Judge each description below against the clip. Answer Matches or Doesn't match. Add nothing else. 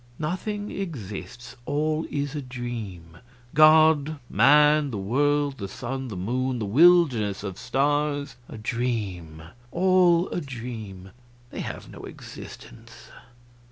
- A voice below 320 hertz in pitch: Matches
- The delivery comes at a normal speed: Doesn't match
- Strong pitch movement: Matches